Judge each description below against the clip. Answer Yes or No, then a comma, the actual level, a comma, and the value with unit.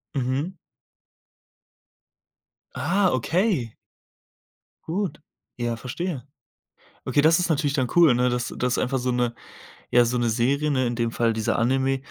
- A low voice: Yes, low, 130 Hz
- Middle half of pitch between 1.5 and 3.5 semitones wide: No, average, 4.1 semitones